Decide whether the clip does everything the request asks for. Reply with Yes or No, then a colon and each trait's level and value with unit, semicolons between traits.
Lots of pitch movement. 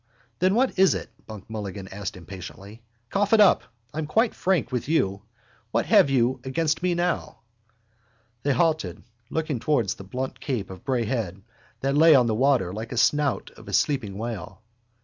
Yes: wide, 7.2 semitones